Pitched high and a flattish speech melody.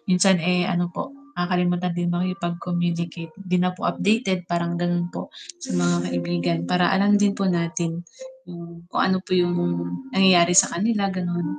No: medium, 175 Hz; narrow, 1.4 semitones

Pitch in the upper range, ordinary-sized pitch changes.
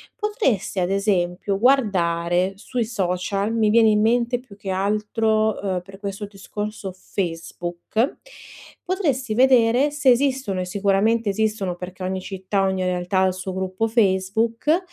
Yes: high, 200 Hz; average, 3.4 semitones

